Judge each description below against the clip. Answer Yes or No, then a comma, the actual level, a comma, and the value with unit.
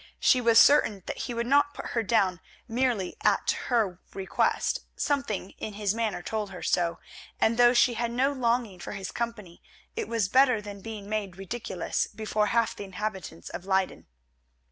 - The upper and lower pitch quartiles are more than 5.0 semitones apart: No, average, 3.7 semitones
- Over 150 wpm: Yes, average, 175 wpm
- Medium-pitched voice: No, high, 215 Hz